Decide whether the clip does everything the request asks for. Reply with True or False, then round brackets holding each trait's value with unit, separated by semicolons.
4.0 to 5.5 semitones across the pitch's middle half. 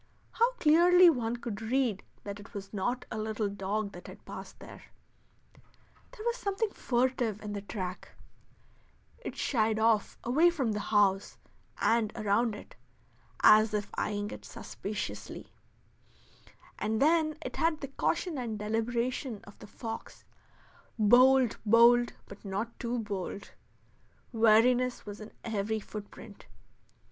False (3.4 semitones)